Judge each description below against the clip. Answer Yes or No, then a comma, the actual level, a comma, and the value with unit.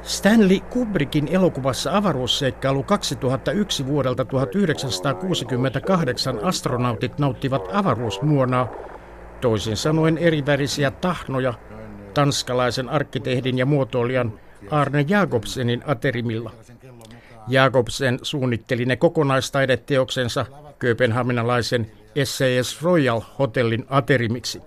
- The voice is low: Yes, low, 130 Hz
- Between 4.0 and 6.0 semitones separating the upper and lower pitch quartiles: No, average, 2.9 semitones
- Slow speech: Yes, slow, 75 wpm